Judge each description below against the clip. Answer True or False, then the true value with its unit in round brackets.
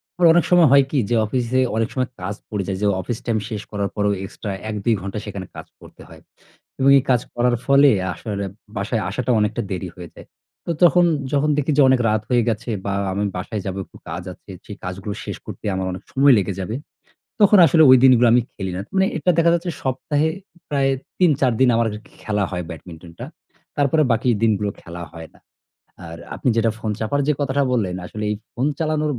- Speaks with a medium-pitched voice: False (115 Hz)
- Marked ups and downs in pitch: True (5.8 semitones)